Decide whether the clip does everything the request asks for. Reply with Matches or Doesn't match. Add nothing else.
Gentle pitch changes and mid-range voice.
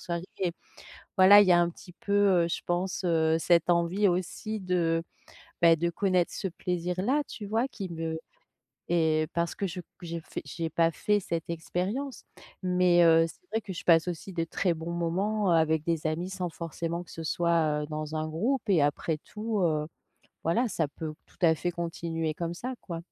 Matches